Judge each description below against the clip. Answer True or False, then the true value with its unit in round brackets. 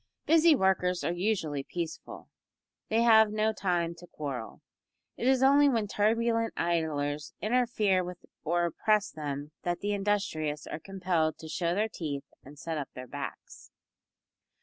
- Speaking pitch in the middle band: True (180 Hz)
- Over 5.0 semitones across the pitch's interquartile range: True (5.6 semitones)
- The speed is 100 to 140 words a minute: False (150 wpm)